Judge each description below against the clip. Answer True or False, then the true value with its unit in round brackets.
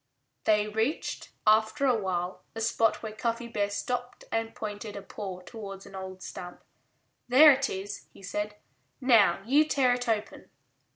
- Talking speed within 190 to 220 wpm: False (160 wpm)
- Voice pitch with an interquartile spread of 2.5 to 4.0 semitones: True (3.6 semitones)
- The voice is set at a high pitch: True (215 Hz)